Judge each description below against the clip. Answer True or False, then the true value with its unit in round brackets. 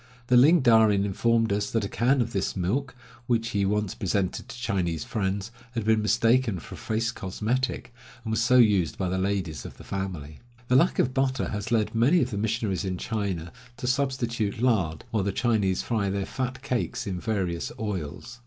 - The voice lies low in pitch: True (110 Hz)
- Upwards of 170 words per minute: True (195 wpm)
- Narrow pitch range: False (3.7 semitones)